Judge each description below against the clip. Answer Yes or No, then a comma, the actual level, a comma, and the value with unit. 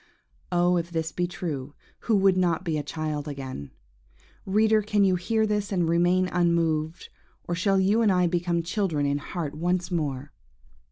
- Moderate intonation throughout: Yes, average, 3.3 semitones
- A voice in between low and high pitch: Yes, medium, 175 Hz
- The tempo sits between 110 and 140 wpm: No, average, 170 wpm